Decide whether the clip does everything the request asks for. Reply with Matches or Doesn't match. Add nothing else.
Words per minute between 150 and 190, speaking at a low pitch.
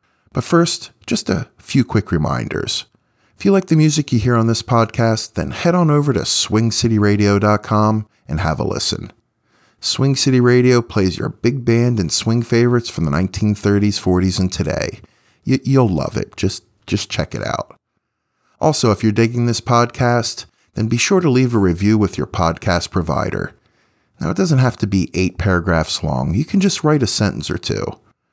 Matches